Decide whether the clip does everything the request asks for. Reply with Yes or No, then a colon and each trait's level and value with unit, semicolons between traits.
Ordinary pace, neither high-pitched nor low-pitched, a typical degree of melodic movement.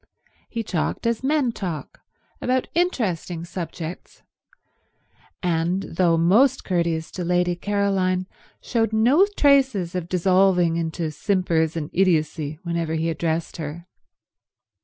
No: slow, 115 wpm; medium, 180 Hz; average, 3.8 semitones